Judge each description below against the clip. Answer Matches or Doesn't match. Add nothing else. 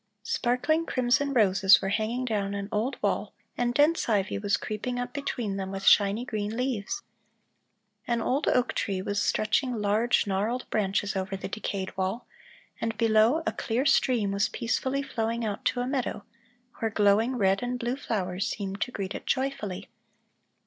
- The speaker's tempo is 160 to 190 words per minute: Matches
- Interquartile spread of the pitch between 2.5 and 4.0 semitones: Matches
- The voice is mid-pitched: Doesn't match